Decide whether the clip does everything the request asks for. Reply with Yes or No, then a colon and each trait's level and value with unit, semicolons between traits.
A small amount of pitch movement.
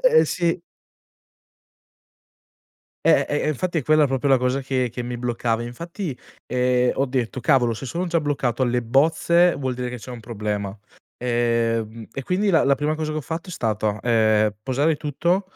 No: average, 4.6 semitones